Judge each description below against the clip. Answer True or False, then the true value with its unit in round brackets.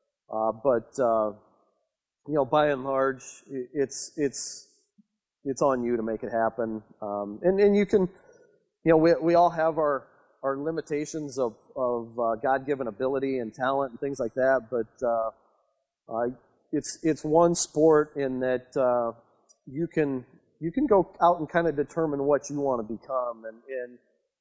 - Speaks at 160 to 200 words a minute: True (170 wpm)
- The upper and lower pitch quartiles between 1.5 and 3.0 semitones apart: False (4.7 semitones)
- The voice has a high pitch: False (135 Hz)